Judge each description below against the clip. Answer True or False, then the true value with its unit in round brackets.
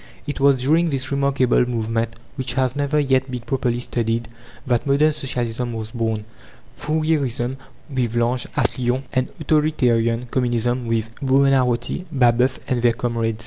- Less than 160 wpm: True (145 wpm)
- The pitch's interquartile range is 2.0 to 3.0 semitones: True (2.7 semitones)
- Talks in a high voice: False (125 Hz)